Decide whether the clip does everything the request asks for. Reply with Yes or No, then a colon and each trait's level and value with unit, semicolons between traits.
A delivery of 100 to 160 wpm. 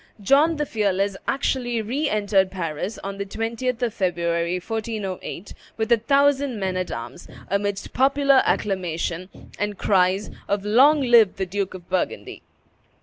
Yes: average, 145 wpm